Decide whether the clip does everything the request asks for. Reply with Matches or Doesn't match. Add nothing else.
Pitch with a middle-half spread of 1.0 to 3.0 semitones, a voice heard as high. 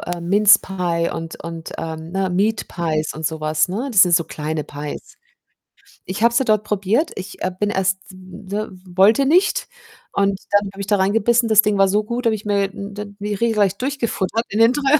Doesn't match